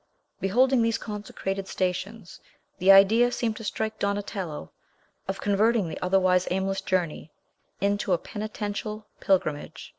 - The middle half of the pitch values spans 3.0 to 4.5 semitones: No, narrow, 2.5 semitones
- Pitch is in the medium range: No, high, 200 Hz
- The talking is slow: Yes, slow, 120 wpm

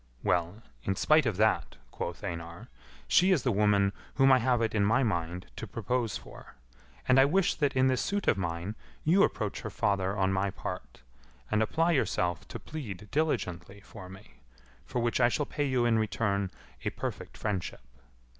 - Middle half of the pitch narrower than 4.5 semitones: No, average, 5.3 semitones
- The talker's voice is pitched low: Yes, low, 105 Hz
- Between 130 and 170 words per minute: No, average, 185 wpm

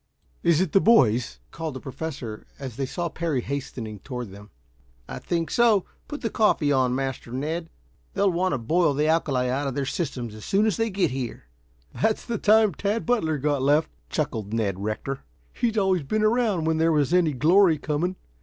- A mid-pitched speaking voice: Yes, medium, 155 Hz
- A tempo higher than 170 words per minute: Yes, average, 190 wpm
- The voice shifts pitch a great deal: Yes, wide, 6.3 semitones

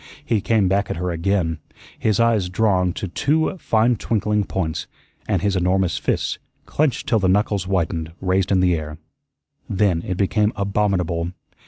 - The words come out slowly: No, average, 160 wpm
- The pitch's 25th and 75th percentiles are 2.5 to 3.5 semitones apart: Yes, average, 2.8 semitones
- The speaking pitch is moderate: No, very low, 95 Hz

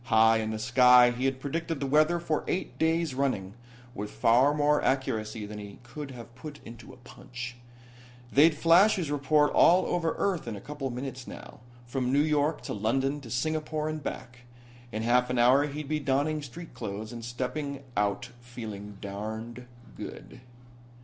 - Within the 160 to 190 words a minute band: Yes, average, 175 wpm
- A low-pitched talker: Yes, low, 130 Hz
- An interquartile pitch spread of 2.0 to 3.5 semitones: No, average, 4.1 semitones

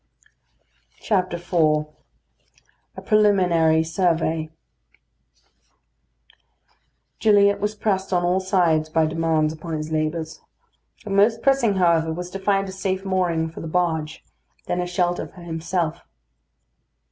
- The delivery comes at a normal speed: No, slow, 115 wpm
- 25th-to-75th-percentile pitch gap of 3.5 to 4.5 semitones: No, average, 3.0 semitones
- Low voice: No, medium, 175 Hz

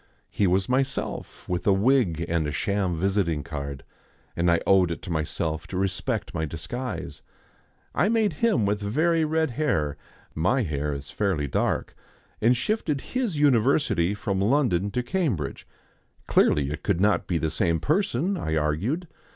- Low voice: Yes, low, 100 Hz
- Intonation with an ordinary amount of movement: No, wide, 8.7 semitones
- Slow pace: No, average, 160 wpm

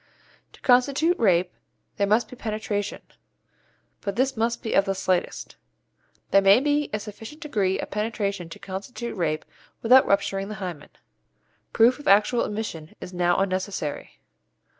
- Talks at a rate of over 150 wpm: No, average, 145 wpm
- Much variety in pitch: No, average, 3.8 semitones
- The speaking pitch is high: Yes, high, 205 Hz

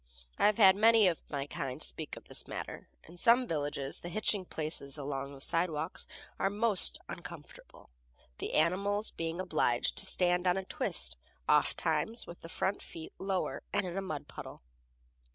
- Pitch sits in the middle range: Yes, medium, 175 Hz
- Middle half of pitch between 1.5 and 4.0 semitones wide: No, average, 4.5 semitones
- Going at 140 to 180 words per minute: Yes, average, 170 wpm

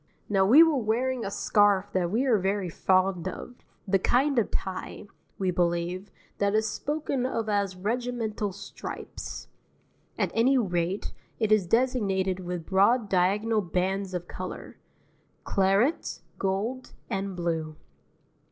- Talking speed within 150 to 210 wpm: No, slow, 135 wpm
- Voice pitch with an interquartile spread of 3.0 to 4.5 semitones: Yes, average, 3.6 semitones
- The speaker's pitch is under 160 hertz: No, high, 200 Hz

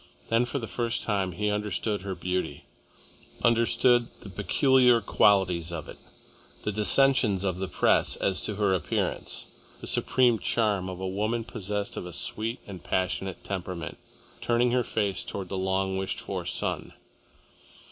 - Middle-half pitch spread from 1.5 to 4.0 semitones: Yes, average, 3.6 semitones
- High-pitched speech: No, low, 100 Hz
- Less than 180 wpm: Yes, average, 155 wpm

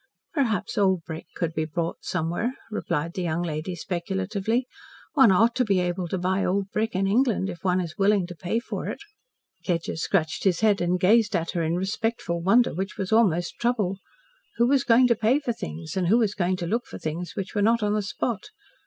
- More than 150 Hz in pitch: Yes, high, 190 Hz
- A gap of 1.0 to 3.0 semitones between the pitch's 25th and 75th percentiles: No, average, 4.2 semitones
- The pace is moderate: No, fast, 215 wpm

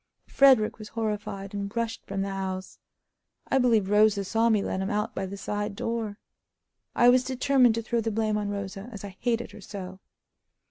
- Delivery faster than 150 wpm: Yes, average, 190 wpm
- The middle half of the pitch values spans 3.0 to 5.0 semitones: No, narrow, 2.5 semitones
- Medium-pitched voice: No, high, 210 Hz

